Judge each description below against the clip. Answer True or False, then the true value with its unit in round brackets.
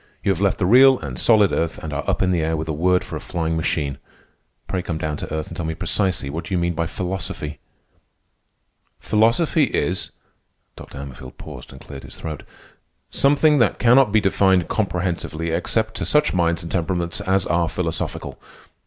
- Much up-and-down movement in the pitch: False (3.7 semitones)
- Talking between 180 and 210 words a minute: True (190 wpm)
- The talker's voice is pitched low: True (85 Hz)